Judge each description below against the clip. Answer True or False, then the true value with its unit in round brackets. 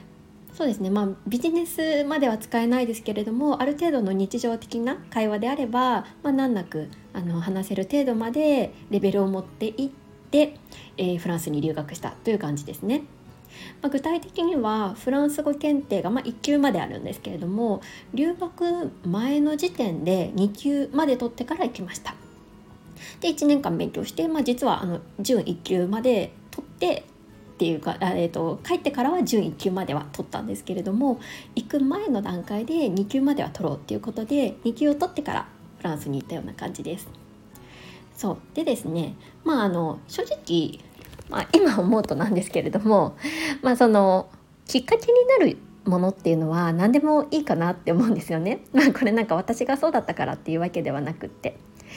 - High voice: True (230 Hz)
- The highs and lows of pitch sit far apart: True (7.3 semitones)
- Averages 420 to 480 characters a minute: False (360 characters per minute)